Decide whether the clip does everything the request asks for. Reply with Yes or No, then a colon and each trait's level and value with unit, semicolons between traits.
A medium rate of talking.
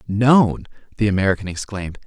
No: slow, 115 wpm